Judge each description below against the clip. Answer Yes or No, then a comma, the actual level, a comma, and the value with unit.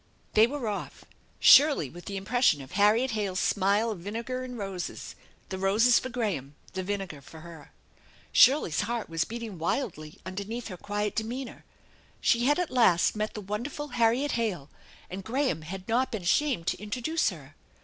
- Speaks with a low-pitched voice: No, high, 210 Hz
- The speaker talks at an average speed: Yes, average, 175 wpm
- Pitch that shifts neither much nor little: Yes, average, 4.7 semitones